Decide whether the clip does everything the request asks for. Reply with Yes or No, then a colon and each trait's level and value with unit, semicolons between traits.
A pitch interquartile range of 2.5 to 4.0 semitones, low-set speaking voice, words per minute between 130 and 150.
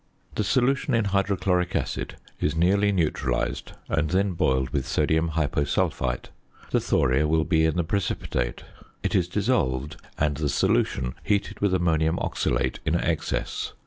No: average, 4.7 semitones; very low, 80 Hz; average, 145 wpm